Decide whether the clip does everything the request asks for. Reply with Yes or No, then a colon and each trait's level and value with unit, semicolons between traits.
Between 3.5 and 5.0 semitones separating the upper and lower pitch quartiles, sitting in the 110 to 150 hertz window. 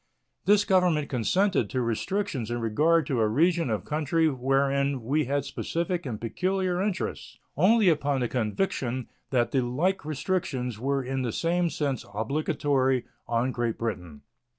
No: wide, 5.6 semitones; medium, 140 Hz